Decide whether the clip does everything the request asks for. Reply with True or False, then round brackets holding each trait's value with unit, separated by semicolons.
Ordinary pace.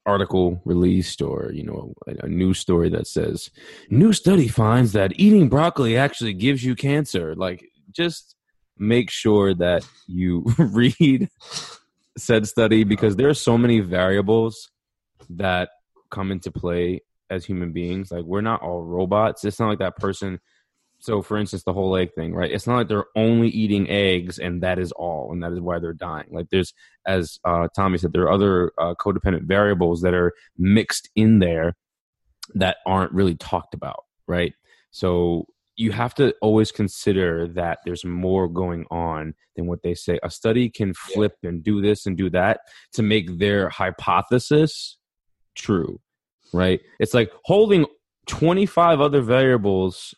True (165 wpm)